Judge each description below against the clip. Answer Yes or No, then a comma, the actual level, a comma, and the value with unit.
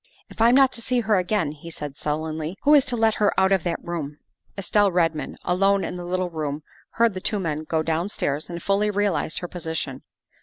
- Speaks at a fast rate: Yes, fast, 220 wpm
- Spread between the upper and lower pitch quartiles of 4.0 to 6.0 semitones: Yes, average, 4.6 semitones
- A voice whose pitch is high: No, medium, 180 Hz